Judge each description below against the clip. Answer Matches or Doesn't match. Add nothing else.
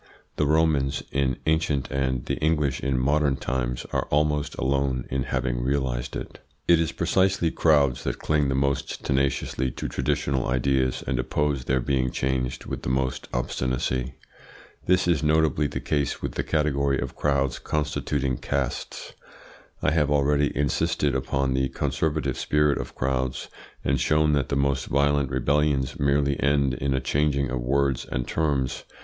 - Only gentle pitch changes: Matches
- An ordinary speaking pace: Matches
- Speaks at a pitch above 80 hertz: Doesn't match